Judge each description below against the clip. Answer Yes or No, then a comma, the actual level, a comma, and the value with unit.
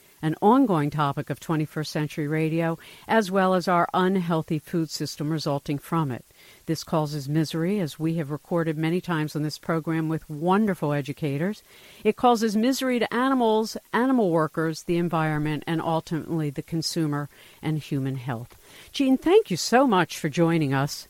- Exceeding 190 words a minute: No, average, 160 wpm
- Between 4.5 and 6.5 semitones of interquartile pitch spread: No, average, 3.5 semitones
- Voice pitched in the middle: Yes, medium, 160 Hz